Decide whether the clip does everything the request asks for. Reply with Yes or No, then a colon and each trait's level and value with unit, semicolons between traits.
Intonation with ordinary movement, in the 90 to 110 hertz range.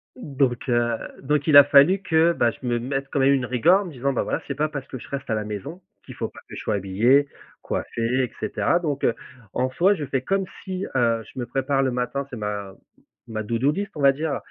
No: average, 3.9 semitones; low, 135 Hz